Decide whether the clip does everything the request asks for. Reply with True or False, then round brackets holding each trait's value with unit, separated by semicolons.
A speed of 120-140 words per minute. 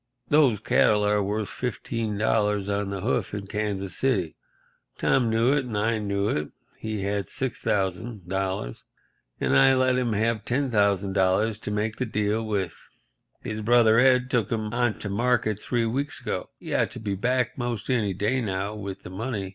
False (170 wpm)